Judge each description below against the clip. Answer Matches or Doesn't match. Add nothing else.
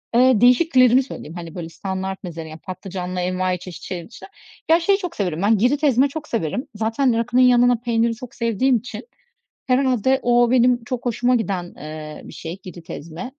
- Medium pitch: Doesn't match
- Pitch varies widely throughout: Matches